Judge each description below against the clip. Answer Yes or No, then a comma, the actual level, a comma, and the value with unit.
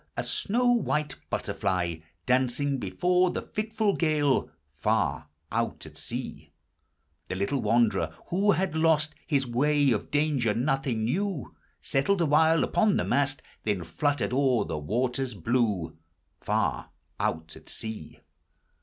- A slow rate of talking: Yes, slow, 130 wpm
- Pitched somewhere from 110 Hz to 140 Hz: Yes, low, 135 Hz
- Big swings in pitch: Yes, wide, 6.0 semitones